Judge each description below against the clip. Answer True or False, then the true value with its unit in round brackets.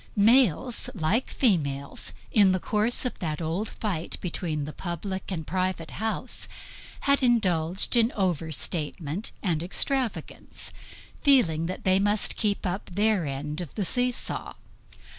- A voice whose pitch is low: False (185 Hz)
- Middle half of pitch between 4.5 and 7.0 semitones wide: True (5.2 semitones)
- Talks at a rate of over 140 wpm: False (135 wpm)